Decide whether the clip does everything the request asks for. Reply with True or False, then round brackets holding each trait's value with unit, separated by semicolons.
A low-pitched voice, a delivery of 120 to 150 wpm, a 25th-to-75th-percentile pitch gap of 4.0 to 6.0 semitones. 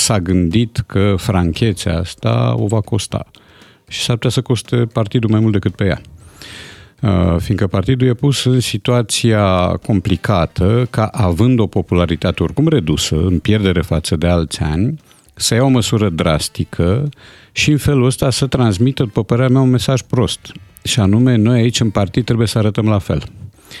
False (110 Hz; 170 wpm; 4.8 semitones)